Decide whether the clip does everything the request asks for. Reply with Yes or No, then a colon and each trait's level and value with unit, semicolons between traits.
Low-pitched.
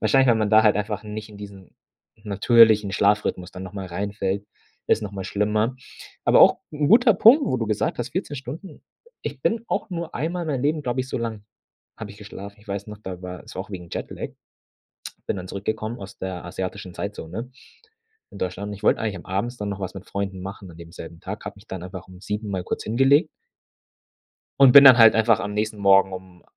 Yes: low, 105 Hz